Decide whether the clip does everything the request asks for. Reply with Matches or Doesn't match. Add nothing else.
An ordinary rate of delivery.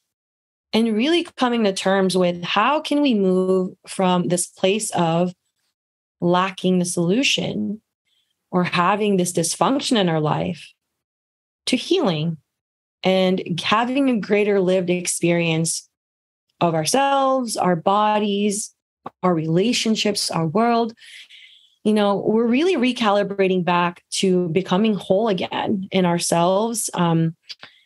Doesn't match